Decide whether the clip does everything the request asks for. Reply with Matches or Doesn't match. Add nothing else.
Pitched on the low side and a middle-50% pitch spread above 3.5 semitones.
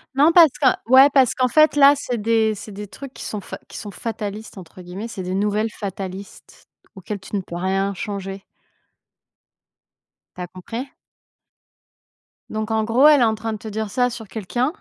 Doesn't match